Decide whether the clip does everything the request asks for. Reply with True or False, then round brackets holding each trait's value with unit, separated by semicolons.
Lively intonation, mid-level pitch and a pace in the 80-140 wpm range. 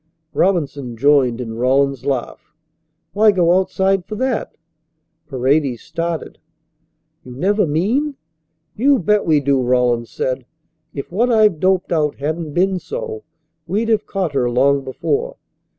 True (7.1 semitones; 160 Hz; 135 wpm)